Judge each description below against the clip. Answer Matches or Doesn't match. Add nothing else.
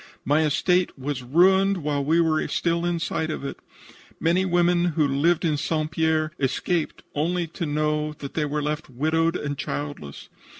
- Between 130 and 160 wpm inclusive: Doesn't match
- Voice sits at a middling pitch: Matches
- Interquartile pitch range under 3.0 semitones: Matches